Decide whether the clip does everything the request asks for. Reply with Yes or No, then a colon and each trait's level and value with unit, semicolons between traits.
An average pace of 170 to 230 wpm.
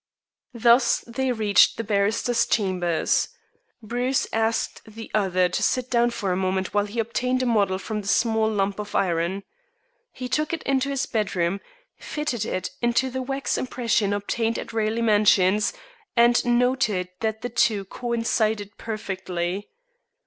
No: average, 150 wpm